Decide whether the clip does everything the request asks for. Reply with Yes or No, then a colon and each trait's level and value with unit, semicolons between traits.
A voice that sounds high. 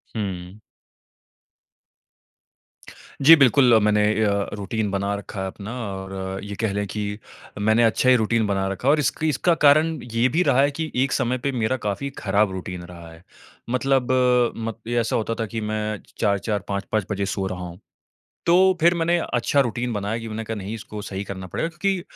No: low, 110 Hz